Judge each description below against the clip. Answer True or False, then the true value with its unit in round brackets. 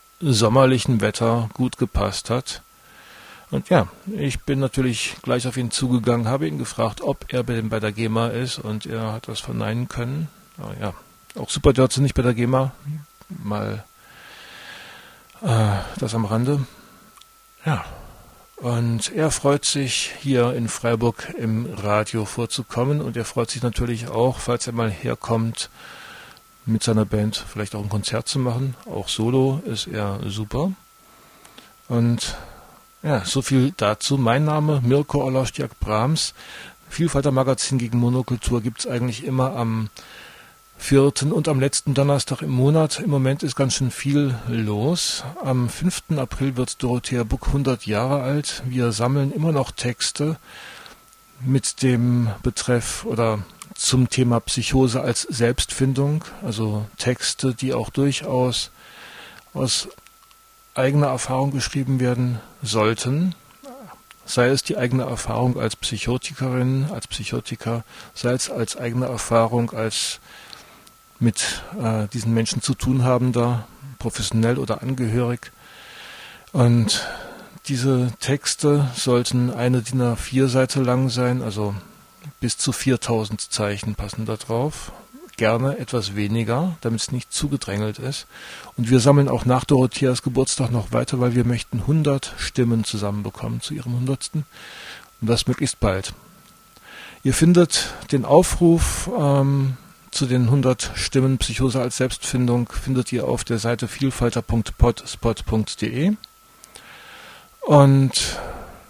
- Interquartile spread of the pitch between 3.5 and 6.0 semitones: False (3.0 semitones)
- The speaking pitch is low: True (125 Hz)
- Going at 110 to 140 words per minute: True (130 wpm)